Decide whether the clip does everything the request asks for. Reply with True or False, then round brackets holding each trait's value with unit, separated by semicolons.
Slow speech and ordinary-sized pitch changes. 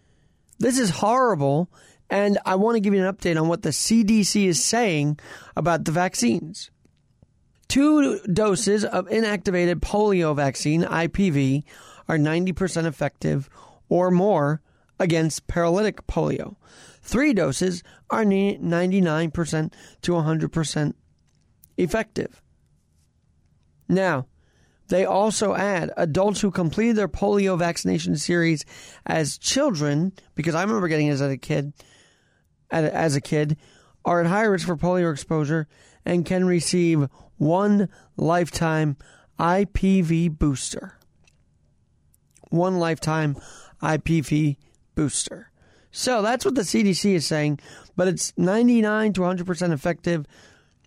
True (115 wpm; 4.3 semitones)